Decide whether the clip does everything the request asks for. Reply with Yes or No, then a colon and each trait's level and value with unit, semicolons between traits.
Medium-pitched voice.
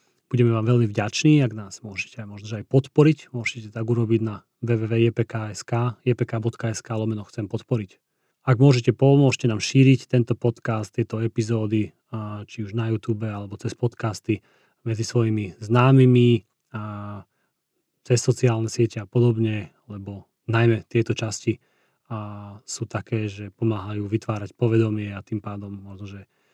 No: low, 115 Hz